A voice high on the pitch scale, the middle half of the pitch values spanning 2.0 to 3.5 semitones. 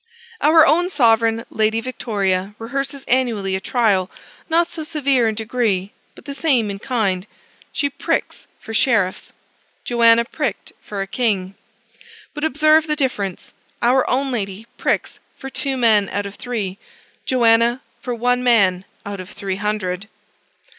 No: high, 230 Hz; average, 4.7 semitones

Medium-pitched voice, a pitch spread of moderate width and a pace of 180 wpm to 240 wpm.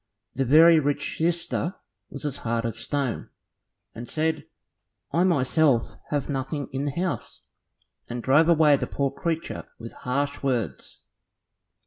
No: medium, 145 Hz; average, 3.7 semitones; average, 140 wpm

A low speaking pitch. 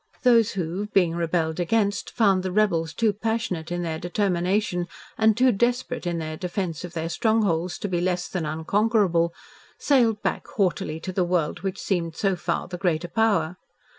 No: medium, 180 Hz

